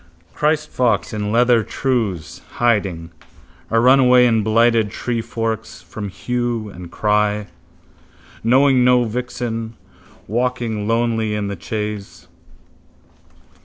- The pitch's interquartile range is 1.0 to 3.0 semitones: Yes, average, 2.7 semitones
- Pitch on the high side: No, low, 115 Hz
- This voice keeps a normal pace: No, slow, 95 wpm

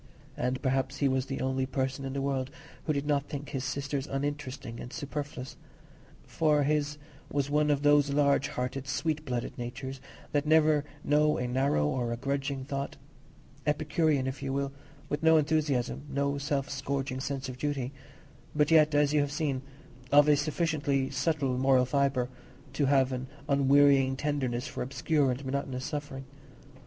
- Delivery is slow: No, average, 165 wpm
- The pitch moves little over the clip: Yes, narrow, 1.8 semitones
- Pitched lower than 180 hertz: Yes, medium, 140 Hz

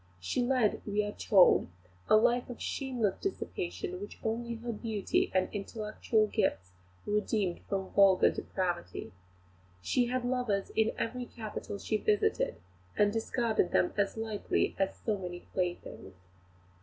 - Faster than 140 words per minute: No, slow, 135 wpm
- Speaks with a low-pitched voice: No, high, 210 Hz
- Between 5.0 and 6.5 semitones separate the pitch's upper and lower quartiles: No, average, 3.3 semitones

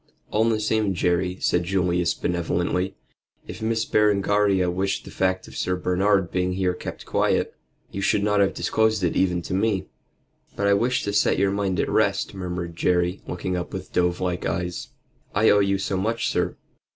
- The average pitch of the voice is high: No, very low, 95 Hz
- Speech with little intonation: Yes, narrow, 2.3 semitones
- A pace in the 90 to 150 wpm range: No, average, 185 wpm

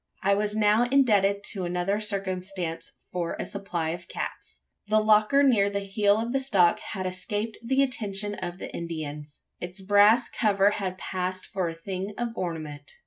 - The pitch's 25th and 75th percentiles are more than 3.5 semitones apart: No, average, 2.9 semitones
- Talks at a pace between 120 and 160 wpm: No, average, 170 wpm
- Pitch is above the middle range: Yes, high, 200 Hz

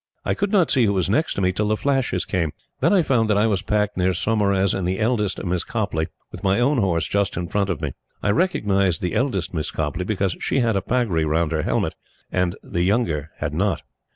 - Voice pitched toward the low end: Yes, very low, 95 Hz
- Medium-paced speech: No, fast, 230 wpm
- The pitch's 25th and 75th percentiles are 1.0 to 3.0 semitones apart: No, average, 4.1 semitones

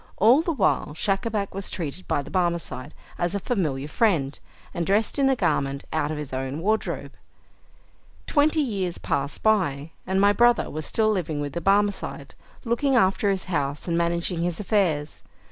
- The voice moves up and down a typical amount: No, wide, 6.1 semitones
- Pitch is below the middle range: No, medium, 185 Hz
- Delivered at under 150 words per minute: No, average, 170 wpm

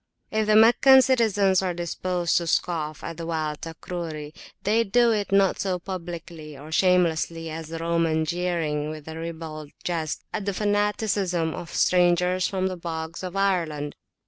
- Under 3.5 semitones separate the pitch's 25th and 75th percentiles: Yes, average, 3.1 semitones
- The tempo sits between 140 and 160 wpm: Yes, average, 155 wpm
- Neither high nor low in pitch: Yes, medium, 175 Hz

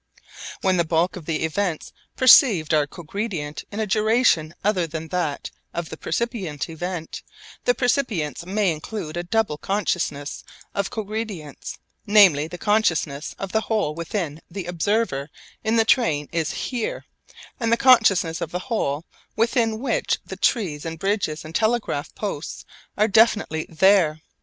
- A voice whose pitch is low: No, medium, 180 Hz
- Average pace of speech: Yes, average, 150 wpm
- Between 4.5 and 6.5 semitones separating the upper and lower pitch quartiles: Yes, wide, 5.5 semitones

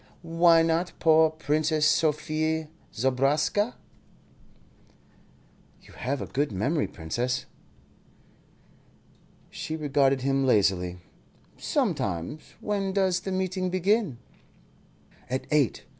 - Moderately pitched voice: Yes, medium, 155 Hz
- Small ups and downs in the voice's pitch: No, average, 4.3 semitones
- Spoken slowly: Yes, slow, 90 wpm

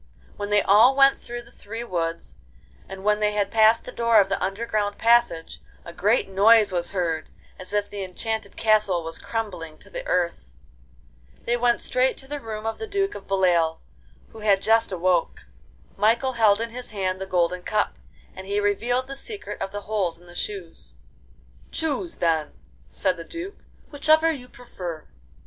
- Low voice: No, high, 205 Hz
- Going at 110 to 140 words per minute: No, average, 180 wpm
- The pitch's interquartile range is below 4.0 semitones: No, average, 4.3 semitones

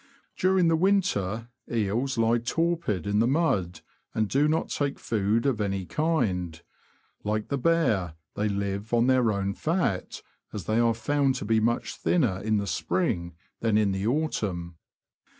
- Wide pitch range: Yes, wide, 6.1 semitones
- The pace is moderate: Yes, average, 160 wpm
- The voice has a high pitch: No, low, 115 Hz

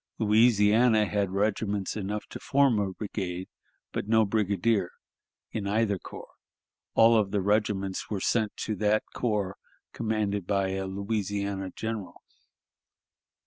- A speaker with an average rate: No, slow, 125 wpm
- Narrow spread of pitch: Yes, narrow, 1.9 semitones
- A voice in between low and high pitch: No, low, 105 Hz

